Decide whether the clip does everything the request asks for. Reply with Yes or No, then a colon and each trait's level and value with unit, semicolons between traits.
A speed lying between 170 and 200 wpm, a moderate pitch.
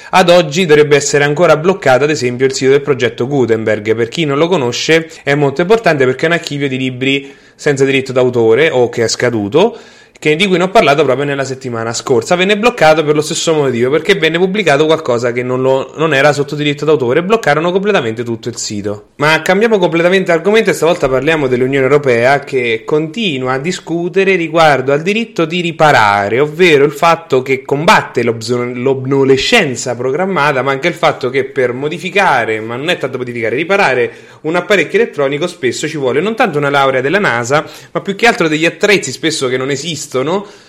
Yes: average, 185 wpm; medium, 150 Hz